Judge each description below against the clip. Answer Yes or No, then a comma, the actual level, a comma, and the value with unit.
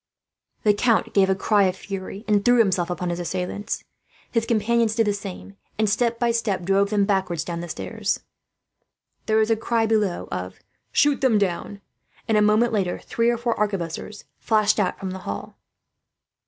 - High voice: Yes, high, 205 Hz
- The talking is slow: No, average, 180 wpm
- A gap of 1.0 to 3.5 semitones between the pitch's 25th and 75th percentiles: Yes, average, 3.0 semitones